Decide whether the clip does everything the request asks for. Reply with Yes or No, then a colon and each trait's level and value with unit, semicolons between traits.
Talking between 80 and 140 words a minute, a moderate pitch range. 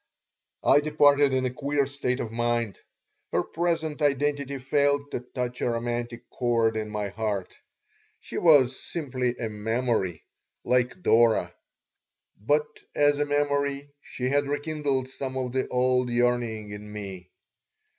Yes: slow, 135 wpm; average, 3.4 semitones